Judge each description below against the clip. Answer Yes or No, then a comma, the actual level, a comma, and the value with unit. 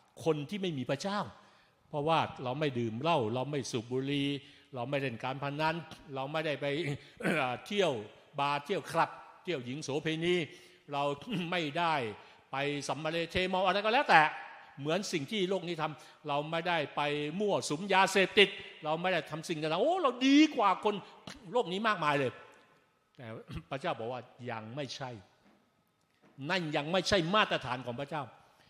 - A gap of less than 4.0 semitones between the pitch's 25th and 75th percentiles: No, average, 4.5 semitones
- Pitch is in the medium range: Yes, medium, 155 Hz